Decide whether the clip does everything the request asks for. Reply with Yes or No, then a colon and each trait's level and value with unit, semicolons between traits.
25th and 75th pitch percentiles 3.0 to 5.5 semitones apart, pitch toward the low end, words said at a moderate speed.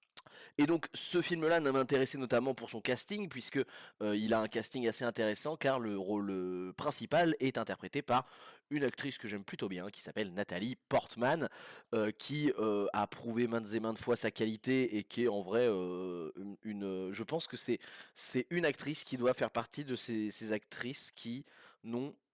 Yes: average, 4.1 semitones; low, 120 Hz; average, 190 wpm